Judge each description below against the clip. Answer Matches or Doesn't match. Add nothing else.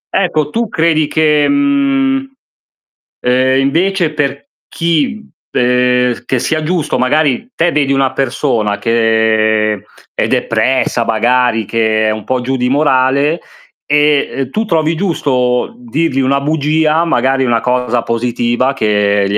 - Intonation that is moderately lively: Matches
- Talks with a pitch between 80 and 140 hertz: Matches